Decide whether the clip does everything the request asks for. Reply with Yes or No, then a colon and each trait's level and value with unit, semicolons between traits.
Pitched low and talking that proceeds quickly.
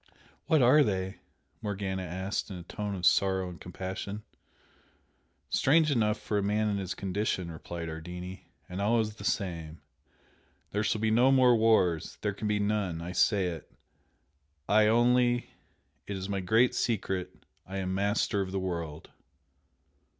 No: low, 100 Hz; average, 155 wpm